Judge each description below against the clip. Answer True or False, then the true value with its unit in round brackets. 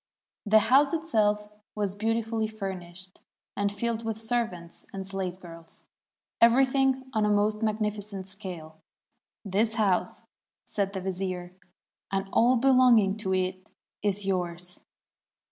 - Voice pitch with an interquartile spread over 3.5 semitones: False (3.1 semitones)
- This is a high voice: True (205 Hz)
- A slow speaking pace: True (125 wpm)